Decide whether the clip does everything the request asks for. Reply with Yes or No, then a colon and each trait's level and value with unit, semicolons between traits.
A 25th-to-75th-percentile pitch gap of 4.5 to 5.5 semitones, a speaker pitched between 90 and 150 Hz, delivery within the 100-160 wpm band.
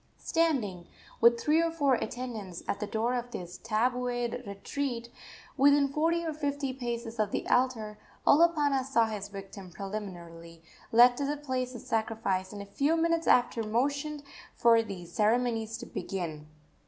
No: average, 5.2 semitones; high, 235 Hz; average, 155 wpm